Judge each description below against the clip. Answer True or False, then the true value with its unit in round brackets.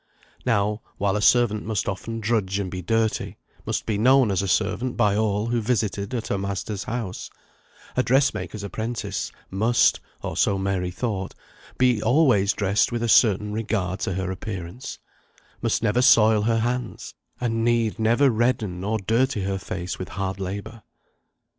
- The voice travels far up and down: False (3.1 semitones)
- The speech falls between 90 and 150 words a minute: False (160 wpm)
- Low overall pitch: True (110 Hz)